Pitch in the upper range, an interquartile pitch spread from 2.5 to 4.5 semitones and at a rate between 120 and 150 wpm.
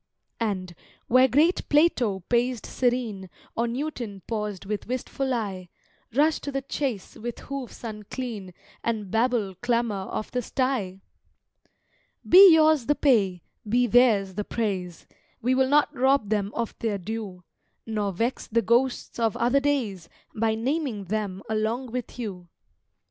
Yes: high, 230 Hz; average, 4.1 semitones; average, 140 wpm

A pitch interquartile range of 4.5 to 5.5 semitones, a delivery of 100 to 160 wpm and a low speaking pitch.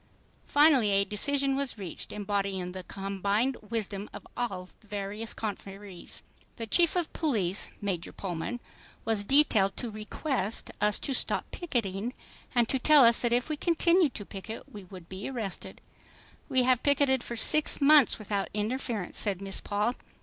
No: average, 5.1 semitones; average, 155 wpm; high, 220 Hz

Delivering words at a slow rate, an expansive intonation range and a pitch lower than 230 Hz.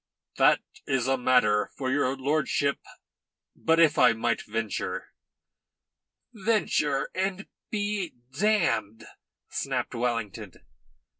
Yes: slow, 100 wpm; wide, 7.1 semitones; low, 135 Hz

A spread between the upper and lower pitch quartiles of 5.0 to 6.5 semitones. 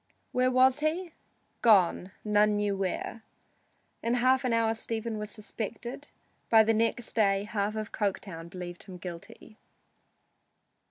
No: average, 3.1 semitones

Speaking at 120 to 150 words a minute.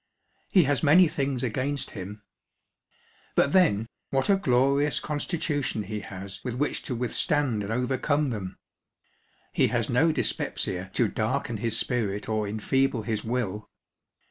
Yes: average, 140 wpm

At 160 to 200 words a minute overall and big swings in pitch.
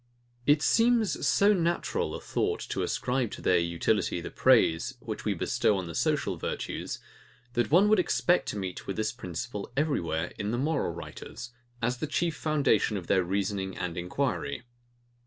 Yes: average, 165 wpm; wide, 8.7 semitones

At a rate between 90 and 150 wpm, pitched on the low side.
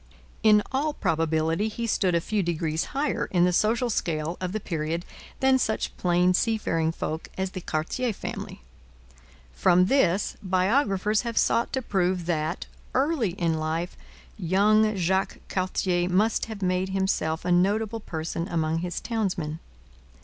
No: average, 145 wpm; medium, 185 Hz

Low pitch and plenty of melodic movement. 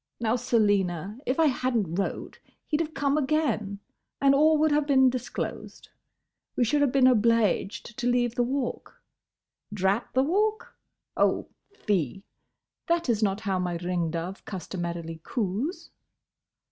No: high, 235 Hz; wide, 6.3 semitones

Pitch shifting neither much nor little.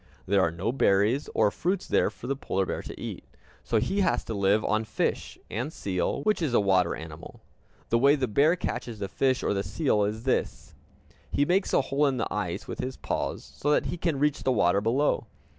No: wide, 6.0 semitones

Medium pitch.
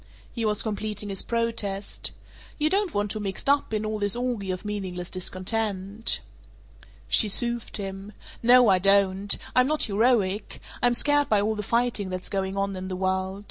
No: high, 205 Hz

